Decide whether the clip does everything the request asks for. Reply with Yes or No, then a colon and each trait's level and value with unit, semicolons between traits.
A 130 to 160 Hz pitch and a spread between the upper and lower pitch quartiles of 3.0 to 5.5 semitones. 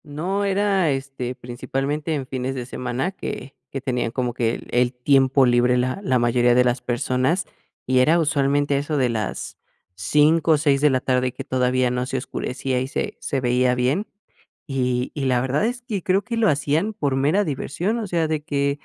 Yes: low, 135 Hz; average, 3.6 semitones